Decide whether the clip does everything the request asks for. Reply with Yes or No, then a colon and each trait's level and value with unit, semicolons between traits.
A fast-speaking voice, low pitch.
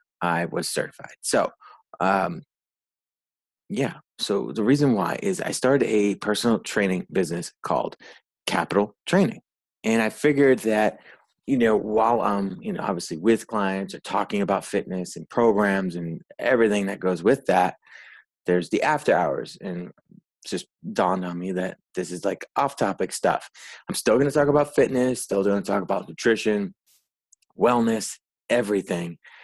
No: average, 155 wpm; low, 105 Hz